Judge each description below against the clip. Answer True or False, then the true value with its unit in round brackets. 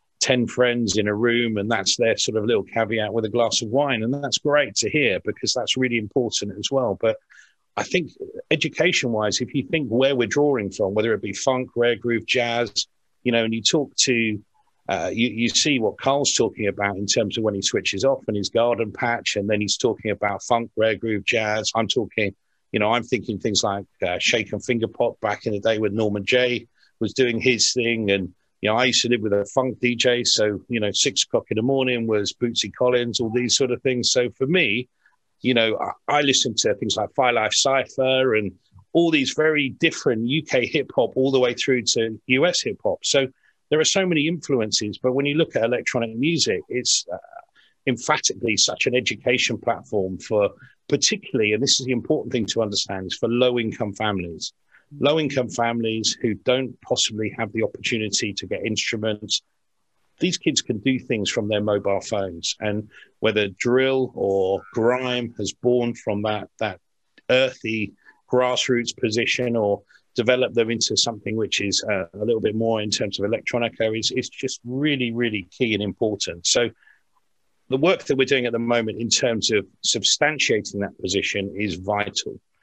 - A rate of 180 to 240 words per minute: True (195 wpm)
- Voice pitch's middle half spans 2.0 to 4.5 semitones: True (3.3 semitones)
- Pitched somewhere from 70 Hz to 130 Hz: True (115 Hz)